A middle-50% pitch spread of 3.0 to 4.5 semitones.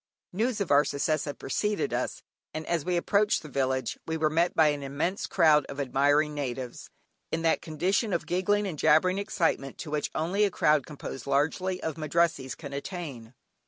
Yes: average, 4.2 semitones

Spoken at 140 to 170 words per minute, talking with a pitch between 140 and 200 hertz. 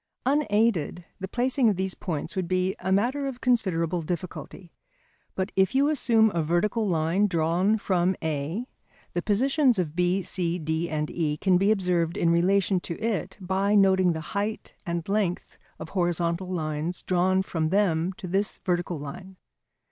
Yes: average, 165 wpm; medium, 185 Hz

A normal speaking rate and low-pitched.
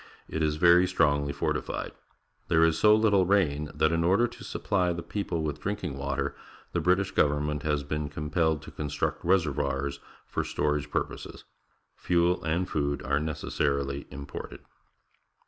Yes: average, 145 wpm; very low, 75 Hz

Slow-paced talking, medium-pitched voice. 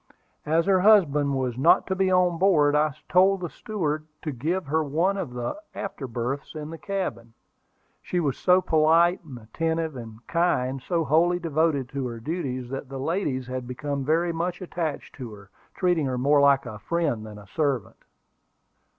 No: average, 175 wpm; medium, 150 Hz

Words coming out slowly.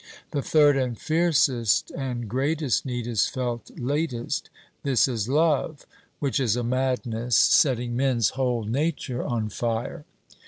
Yes: slow, 130 wpm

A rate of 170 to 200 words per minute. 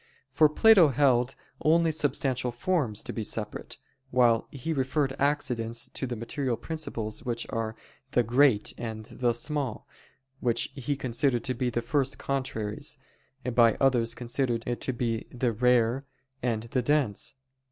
No: average, 140 wpm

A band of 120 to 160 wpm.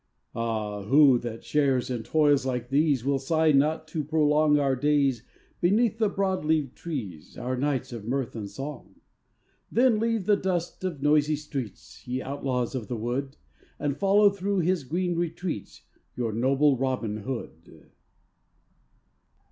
Yes: average, 150 wpm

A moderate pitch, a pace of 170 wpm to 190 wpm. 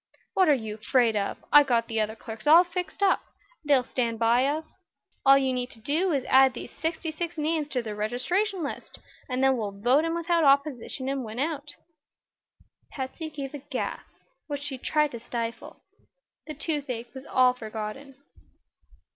No: very high, 270 Hz; average, 175 wpm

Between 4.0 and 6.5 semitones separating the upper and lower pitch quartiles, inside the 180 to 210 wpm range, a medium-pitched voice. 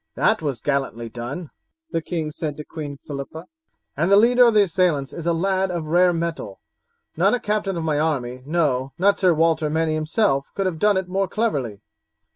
Yes: average, 4.6 semitones; average, 195 wpm; medium, 165 Hz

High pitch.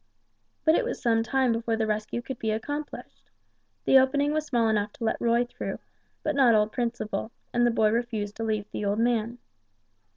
Yes: high, 230 Hz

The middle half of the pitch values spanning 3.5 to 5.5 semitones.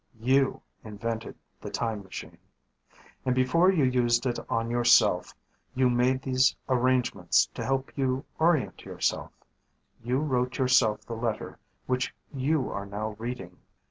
No: narrow, 2.4 semitones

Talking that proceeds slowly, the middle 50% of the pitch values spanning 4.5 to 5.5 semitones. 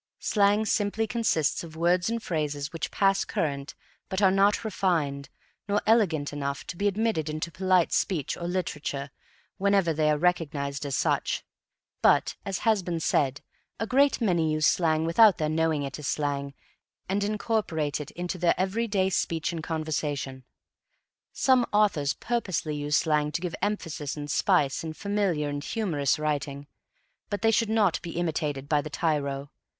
No: average, 160 wpm; average, 5.2 semitones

